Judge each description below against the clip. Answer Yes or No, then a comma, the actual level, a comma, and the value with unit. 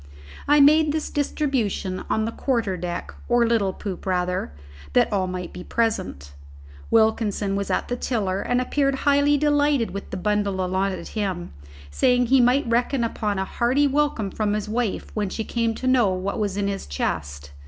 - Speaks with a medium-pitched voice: No, high, 220 Hz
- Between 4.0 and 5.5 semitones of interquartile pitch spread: Yes, average, 4.9 semitones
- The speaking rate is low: No, average, 180 wpm